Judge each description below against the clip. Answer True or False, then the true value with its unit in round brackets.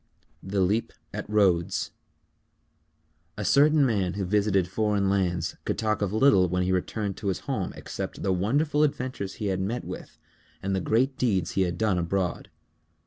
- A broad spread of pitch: False (3.1 semitones)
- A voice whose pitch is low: True (100 Hz)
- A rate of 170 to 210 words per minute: True (175 wpm)